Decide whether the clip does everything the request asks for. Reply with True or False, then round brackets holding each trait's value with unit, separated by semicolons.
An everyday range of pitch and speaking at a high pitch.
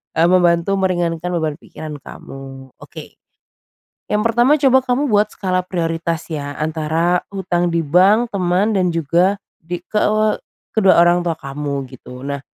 False (3.6 semitones; 175 Hz)